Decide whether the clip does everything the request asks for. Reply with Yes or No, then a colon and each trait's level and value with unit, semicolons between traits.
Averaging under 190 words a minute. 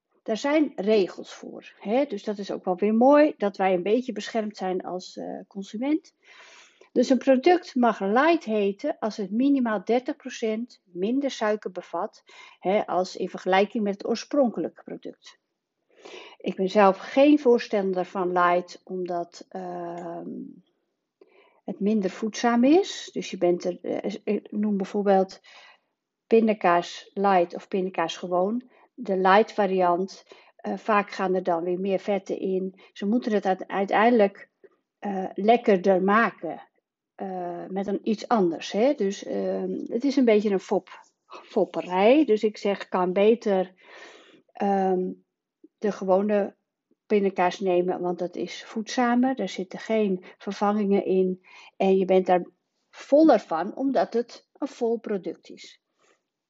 Yes: average, 140 wpm